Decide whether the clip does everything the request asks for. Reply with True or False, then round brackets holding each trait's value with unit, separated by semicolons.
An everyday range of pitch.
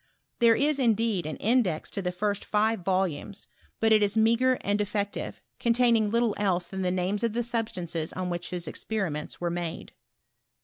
True (4.0 semitones)